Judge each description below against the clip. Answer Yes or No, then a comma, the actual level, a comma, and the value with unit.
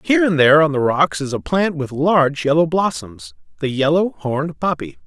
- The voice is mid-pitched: Yes, medium, 155 Hz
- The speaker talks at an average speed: Yes, average, 190 wpm